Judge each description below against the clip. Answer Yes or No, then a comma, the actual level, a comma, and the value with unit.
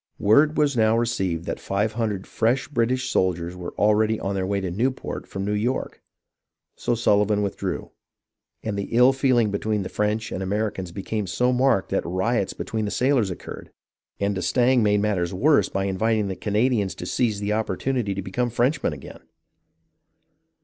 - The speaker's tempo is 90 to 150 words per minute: No, average, 170 wpm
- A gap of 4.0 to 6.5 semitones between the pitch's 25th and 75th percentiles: No, average, 3.6 semitones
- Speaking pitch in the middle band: No, low, 105 Hz